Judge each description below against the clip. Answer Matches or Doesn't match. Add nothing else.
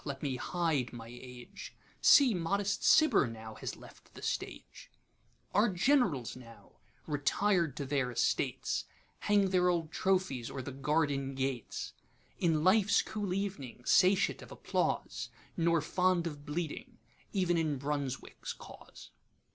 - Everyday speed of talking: Doesn't match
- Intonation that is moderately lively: Doesn't match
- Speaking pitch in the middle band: Matches